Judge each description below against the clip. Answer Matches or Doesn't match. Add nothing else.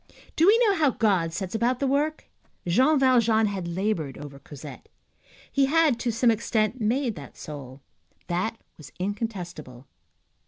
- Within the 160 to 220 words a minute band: Doesn't match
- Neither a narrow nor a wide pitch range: Doesn't match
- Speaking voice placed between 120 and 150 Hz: Doesn't match